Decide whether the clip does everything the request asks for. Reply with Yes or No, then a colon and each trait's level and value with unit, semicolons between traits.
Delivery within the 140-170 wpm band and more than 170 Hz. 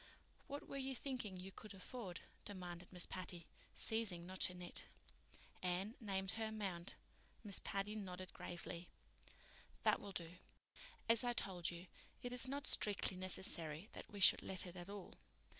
Yes: average, 160 wpm; high, 190 Hz